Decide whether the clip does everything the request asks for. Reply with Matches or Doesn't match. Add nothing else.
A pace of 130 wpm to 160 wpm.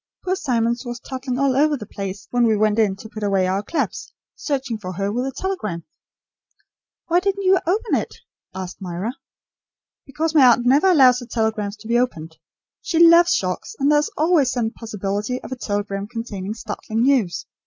Doesn't match